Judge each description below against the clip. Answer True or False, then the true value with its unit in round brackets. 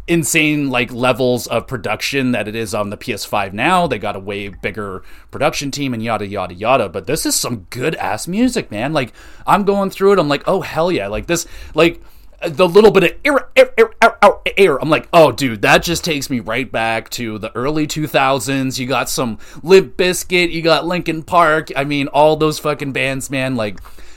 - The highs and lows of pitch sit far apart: True (6.0 semitones)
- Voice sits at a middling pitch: True (145 Hz)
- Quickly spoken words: True (210 wpm)